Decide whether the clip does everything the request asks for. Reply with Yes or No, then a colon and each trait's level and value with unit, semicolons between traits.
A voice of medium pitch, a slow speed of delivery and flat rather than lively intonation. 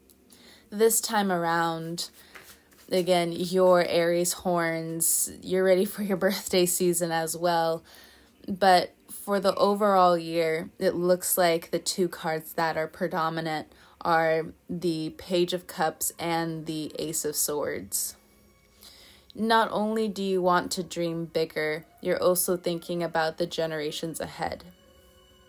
Yes: medium, 170 Hz; slow, 125 wpm; narrow, 2.1 semitones